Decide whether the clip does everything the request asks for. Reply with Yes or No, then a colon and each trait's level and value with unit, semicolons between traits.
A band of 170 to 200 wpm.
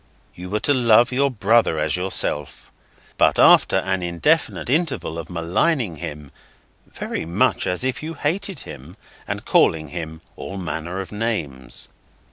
No: average, 145 wpm